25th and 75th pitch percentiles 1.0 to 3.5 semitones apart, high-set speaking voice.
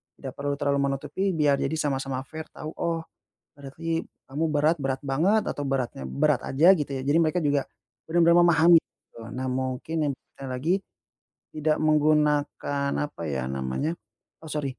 No: average, 2.9 semitones; medium, 145 Hz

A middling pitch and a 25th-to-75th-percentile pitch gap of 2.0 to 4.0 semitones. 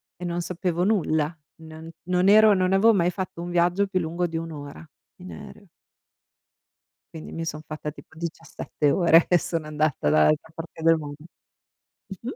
Yes: medium, 165 Hz; narrow, 2.4 semitones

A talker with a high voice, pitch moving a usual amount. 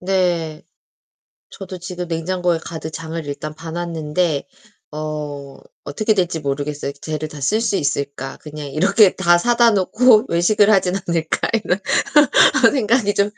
No: medium, 170 Hz; average, 4.2 semitones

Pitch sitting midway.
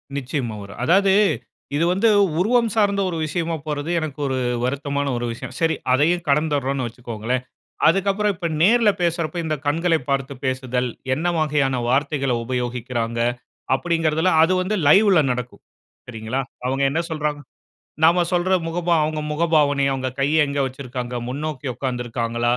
Yes: medium, 145 Hz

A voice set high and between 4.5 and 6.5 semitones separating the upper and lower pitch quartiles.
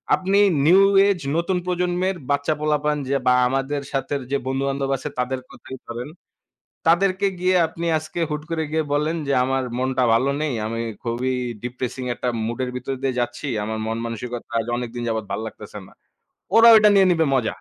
No: low, 135 Hz; average, 5.0 semitones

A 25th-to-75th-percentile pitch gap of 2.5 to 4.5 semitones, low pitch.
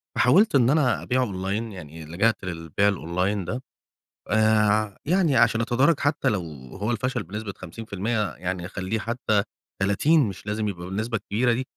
Yes: average, 4.0 semitones; low, 110 Hz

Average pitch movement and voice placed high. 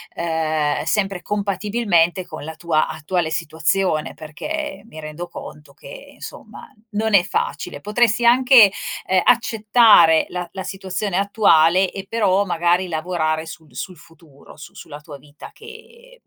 No: average, 4.8 semitones; medium, 180 Hz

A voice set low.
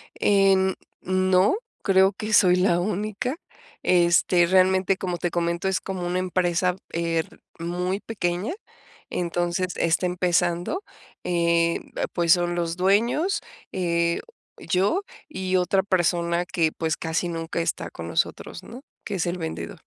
No: medium, 180 Hz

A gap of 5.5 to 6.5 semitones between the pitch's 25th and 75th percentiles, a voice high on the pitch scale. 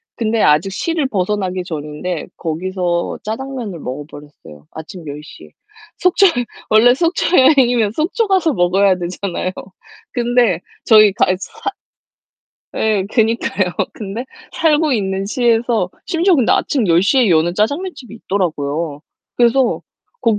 Yes: wide, 6.0 semitones; high, 210 Hz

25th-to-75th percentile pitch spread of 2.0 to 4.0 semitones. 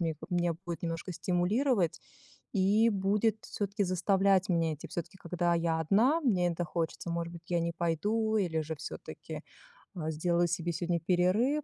Yes: average, 3.0 semitones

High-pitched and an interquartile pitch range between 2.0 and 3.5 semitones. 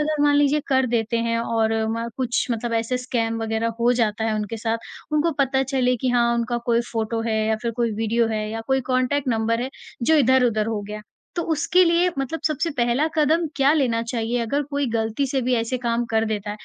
Yes: high, 240 Hz; average, 2.9 semitones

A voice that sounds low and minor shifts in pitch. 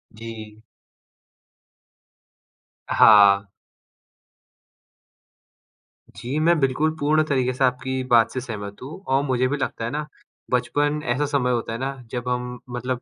No: low, 125 Hz; average, 3.4 semitones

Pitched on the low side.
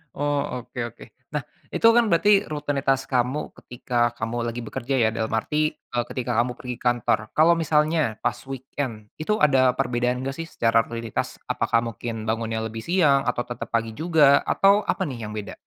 Yes: low, 125 Hz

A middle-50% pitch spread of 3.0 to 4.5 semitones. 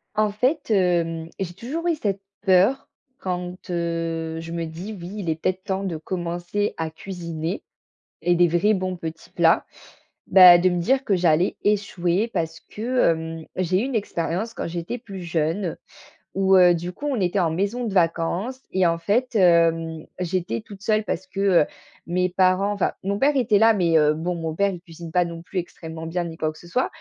Yes: average, 3.3 semitones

